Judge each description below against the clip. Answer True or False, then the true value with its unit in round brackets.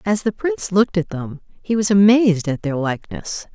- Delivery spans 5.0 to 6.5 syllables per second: True (5.5 syllables/s)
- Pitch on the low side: False (195 Hz)